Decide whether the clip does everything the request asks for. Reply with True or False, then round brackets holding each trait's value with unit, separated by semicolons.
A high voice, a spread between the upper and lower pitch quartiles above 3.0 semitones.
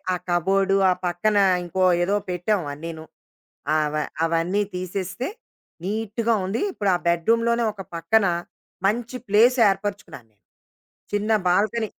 True (195 Hz; 3.8 semitones)